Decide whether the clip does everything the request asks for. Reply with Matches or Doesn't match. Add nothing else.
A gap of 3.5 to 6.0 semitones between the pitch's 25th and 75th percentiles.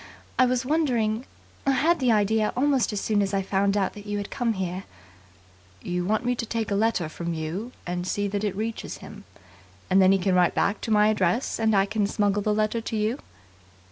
Doesn't match